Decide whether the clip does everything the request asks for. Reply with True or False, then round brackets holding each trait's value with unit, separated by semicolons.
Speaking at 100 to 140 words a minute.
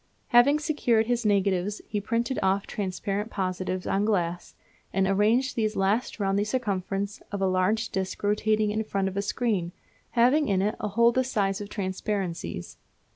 False (175 wpm)